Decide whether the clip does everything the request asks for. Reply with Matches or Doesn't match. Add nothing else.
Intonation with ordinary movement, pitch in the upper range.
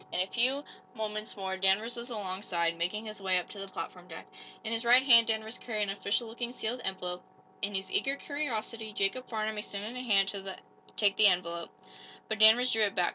Matches